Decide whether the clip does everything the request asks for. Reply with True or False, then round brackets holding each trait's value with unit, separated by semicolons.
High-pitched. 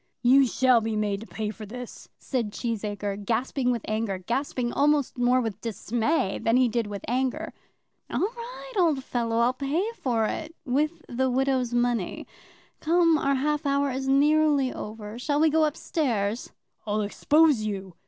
True (250 Hz)